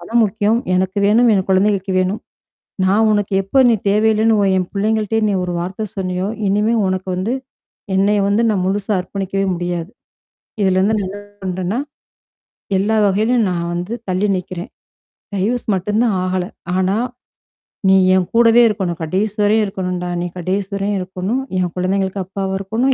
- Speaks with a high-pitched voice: Yes, high, 195 Hz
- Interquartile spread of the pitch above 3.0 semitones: No, narrow, 2.5 semitones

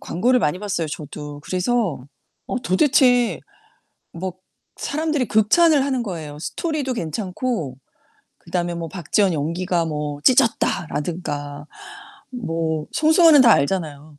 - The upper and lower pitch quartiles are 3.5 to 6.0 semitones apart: No, wide, 8.1 semitones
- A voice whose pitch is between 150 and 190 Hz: Yes, medium, 185 Hz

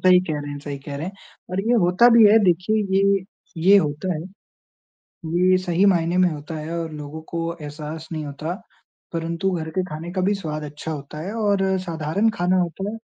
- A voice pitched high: No, medium, 170 Hz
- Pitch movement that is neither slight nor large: Yes, average, 3.5 semitones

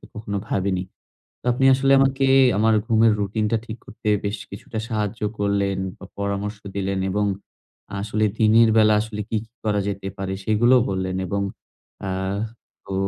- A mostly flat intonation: Yes, narrow, 2.0 semitones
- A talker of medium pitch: No, low, 105 Hz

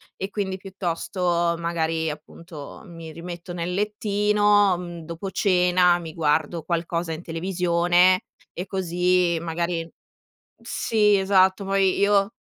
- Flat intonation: Yes, narrow, 2.3 semitones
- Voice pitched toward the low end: No, medium, 180 Hz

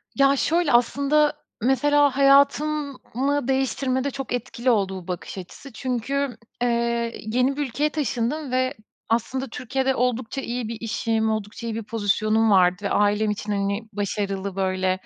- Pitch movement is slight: No, average, 4.3 semitones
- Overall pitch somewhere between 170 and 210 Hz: No, high, 240 Hz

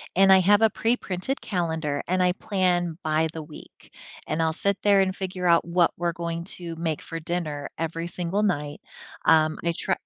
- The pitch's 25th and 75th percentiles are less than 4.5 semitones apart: Yes, narrow, 2.6 semitones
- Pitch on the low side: No, medium, 175 Hz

